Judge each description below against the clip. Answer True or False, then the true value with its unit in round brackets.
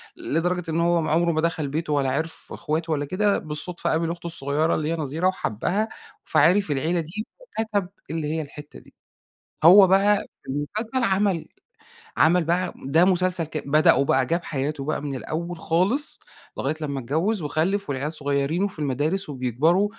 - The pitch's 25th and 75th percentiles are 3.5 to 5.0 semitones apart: True (3.8 semitones)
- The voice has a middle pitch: True (165 Hz)